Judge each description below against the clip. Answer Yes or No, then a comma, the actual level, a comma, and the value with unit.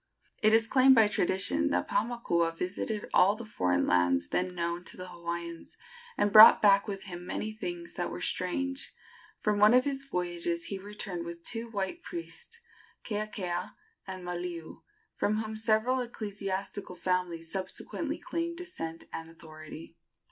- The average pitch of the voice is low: No, high, 190 Hz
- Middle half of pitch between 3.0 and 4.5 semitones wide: Yes, average, 4.2 semitones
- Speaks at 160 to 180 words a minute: No, average, 150 wpm